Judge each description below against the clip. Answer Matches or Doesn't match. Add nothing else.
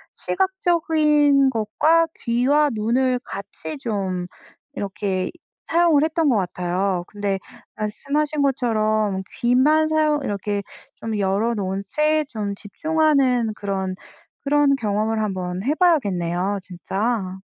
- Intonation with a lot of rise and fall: Matches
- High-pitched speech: Matches